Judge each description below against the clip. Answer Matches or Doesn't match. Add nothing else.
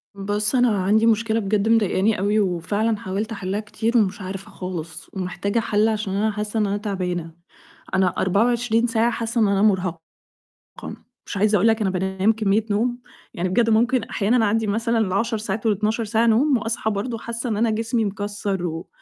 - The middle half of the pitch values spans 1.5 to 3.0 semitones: Matches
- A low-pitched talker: Doesn't match